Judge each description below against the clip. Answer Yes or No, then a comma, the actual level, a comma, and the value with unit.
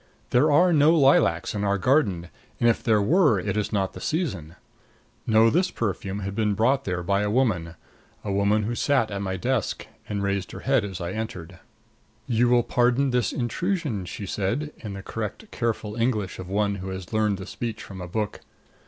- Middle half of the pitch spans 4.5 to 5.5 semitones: No, average, 4.1 semitones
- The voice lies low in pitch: Yes, low, 105 Hz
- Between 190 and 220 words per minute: Yes, average, 195 wpm